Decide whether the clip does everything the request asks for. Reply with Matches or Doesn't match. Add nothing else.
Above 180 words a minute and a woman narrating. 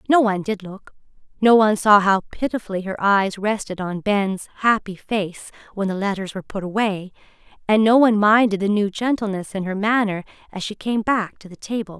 Matches